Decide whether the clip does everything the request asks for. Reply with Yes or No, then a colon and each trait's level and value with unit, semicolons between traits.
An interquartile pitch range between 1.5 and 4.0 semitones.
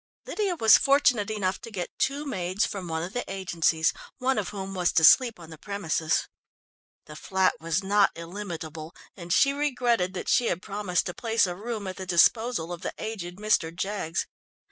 No: average, 4.4 semitones